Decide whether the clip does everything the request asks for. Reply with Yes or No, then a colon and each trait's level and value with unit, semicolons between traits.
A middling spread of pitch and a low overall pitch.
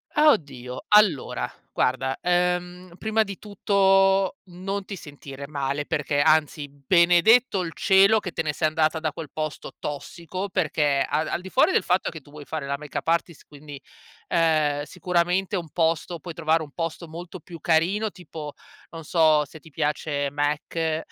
No: average, 3.7 semitones; medium, 165 Hz